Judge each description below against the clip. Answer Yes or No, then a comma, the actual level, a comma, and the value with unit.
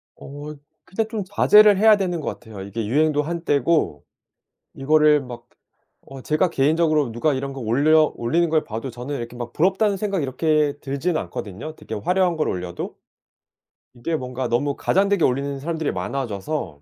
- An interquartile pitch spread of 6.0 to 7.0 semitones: No, average, 5.2 semitones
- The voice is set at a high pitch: No, medium, 145 Hz